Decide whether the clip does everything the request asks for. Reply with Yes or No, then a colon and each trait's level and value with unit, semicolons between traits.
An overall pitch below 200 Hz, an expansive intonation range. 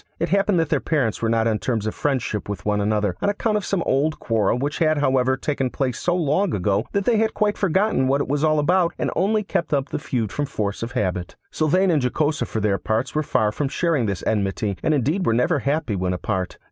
Yes: medium, 140 Hz; wide, 7.0 semitones